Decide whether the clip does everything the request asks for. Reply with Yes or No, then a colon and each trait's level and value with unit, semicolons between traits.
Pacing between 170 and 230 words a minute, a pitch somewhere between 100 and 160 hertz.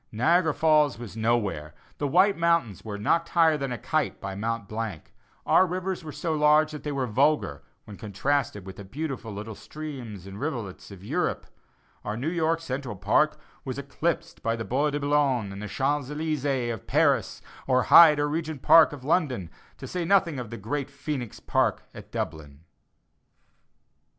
Yes: average, 175 wpm; low, 135 Hz